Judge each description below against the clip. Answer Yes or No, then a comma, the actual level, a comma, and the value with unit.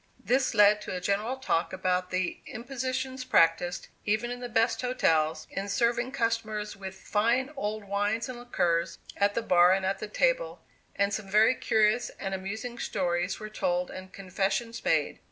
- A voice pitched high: Yes, high, 210 Hz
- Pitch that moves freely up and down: No, average, 4.2 semitones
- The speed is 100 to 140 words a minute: No, average, 170 wpm